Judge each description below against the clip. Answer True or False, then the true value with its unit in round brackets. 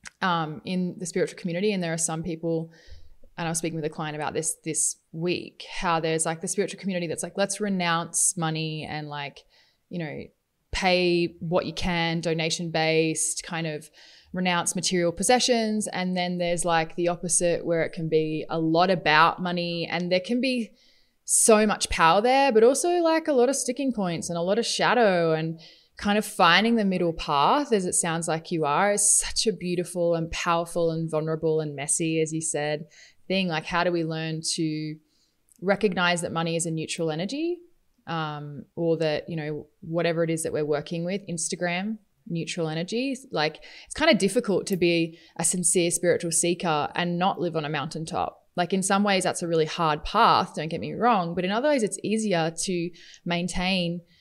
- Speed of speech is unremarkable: True (195 wpm)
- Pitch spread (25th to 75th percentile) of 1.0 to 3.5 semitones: True (2.8 semitones)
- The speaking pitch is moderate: True (170 Hz)